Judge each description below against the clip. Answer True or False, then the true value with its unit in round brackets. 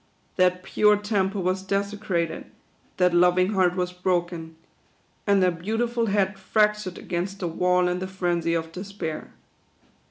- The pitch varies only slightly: True (2.0 semitones)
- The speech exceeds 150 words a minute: False (135 wpm)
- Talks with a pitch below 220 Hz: True (185 Hz)